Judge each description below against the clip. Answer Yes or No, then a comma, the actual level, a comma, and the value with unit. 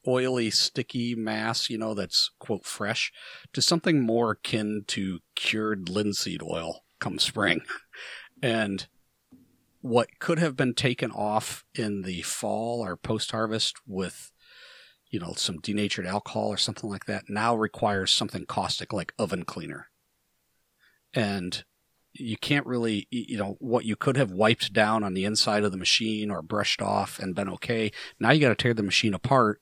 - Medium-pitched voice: No, low, 110 Hz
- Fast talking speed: No, average, 160 wpm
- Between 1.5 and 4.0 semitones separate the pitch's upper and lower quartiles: Yes, average, 2.7 semitones